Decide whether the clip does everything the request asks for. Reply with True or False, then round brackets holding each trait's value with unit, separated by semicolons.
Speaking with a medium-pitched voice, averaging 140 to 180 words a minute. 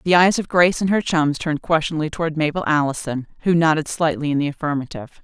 False (155 Hz; 205 wpm)